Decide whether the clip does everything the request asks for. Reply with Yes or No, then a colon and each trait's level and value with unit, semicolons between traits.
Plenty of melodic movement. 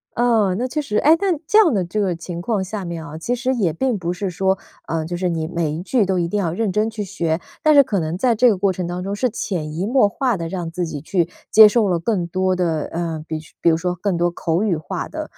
No: average, 4.2 semitones